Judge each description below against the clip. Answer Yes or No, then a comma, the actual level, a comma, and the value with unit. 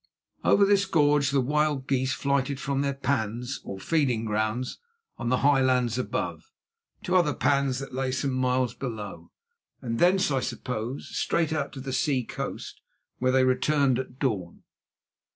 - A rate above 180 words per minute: No, average, 160 wpm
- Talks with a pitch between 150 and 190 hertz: No, low, 130 Hz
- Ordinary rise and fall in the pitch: No, narrow, 2.2 semitones